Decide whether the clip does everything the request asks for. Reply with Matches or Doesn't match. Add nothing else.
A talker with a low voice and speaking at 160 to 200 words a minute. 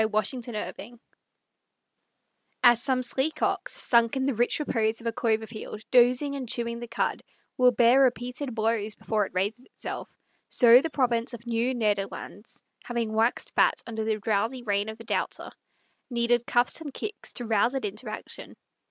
Doesn't match